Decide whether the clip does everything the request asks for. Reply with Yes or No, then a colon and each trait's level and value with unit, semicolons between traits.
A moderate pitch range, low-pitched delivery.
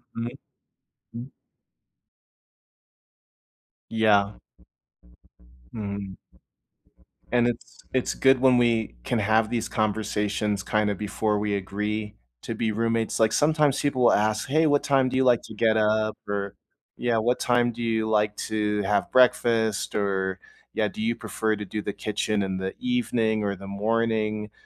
No: narrow, 2.2 semitones; low, 110 Hz